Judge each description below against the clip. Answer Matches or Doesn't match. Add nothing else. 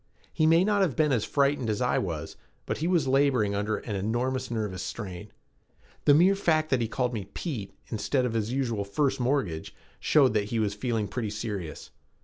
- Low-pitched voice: Matches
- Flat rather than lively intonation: Doesn't match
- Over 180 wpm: Matches